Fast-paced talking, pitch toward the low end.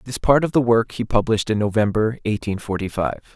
Yes: fast, 215 wpm; low, 110 Hz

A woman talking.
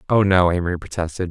No: male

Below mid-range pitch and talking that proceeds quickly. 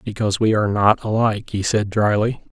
No: low, 105 Hz; average, 190 wpm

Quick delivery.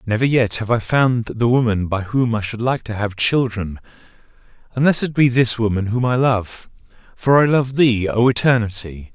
No: average, 190 wpm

